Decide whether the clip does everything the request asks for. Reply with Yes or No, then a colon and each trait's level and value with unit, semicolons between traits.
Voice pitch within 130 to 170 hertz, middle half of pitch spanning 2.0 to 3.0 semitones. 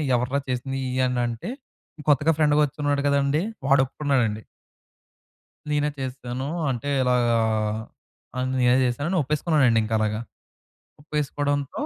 Yes: low, 135 Hz; average, 2.7 semitones